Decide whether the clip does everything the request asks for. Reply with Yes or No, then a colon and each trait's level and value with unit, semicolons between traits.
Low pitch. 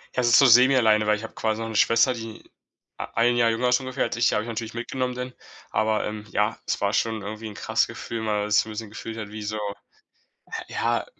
Yes: low, 115 Hz